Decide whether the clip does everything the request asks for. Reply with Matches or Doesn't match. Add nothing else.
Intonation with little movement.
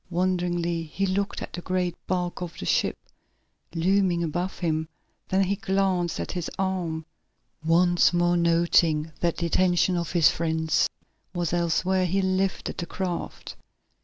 Matches